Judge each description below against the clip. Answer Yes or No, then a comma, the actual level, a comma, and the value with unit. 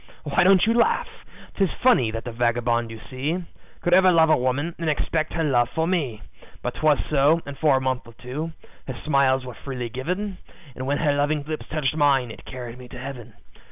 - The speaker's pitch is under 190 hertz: Yes, medium, 140 Hz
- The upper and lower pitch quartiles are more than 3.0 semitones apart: Yes, average, 4.4 semitones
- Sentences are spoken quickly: Yes, fast, 210 wpm